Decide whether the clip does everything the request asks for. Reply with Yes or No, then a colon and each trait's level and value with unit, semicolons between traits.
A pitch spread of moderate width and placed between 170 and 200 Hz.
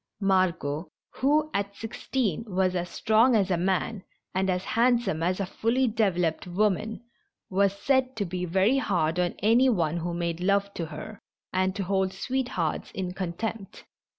Yes: average, 3.8 semitones; high, 190 Hz